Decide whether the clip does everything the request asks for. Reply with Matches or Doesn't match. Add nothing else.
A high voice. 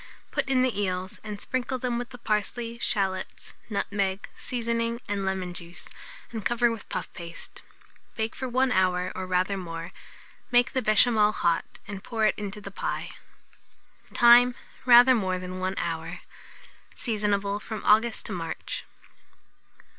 Matches